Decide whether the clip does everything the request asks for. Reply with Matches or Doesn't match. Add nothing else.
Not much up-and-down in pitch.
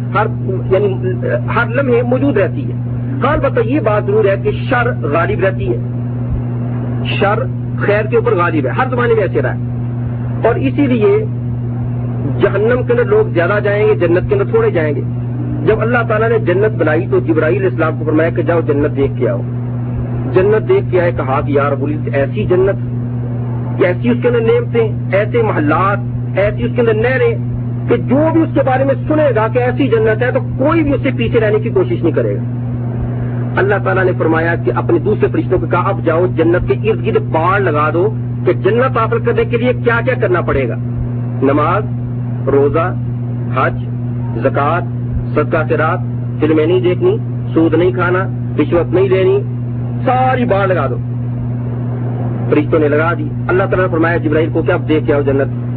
Matches